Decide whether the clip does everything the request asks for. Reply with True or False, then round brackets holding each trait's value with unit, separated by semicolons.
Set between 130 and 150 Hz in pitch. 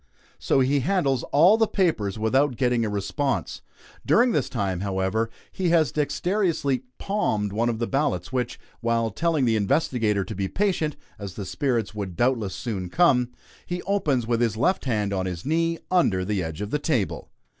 False (120 Hz)